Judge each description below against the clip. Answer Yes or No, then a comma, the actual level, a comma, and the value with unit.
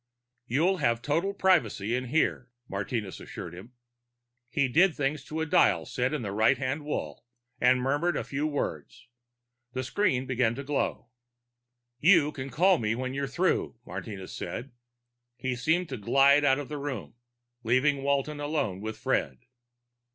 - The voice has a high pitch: No, low, 135 Hz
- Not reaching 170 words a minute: Yes, average, 160 wpm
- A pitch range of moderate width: Yes, average, 4.1 semitones